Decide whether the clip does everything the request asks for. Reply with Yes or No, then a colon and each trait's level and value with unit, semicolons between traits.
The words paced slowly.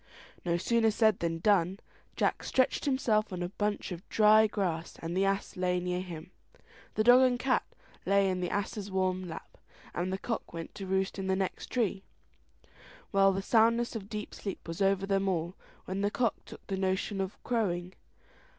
No: average, 185 wpm